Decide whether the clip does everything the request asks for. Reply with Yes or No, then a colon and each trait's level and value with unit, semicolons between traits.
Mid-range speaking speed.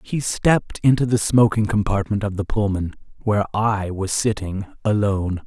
Yes: average, 155 wpm